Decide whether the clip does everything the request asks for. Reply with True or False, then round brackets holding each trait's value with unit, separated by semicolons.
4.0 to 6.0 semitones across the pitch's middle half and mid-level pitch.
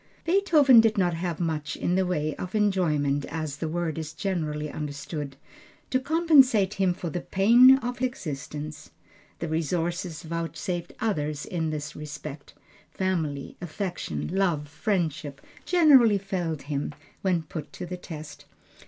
True (4.4 semitones; 170 Hz)